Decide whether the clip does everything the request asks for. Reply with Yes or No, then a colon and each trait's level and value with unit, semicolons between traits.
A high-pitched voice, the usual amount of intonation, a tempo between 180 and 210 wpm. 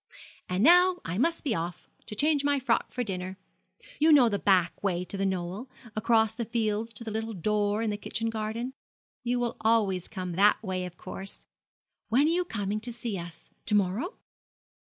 Yes: high, 215 Hz; average, 3.9 semitones; average, 195 wpm